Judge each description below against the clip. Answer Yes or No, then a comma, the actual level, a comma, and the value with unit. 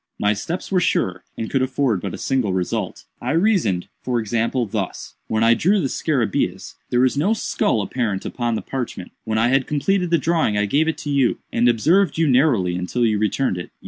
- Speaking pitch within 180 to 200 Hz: No, low, 125 Hz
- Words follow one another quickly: Yes, fast, 210 wpm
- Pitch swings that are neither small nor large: No, wide, 5.7 semitones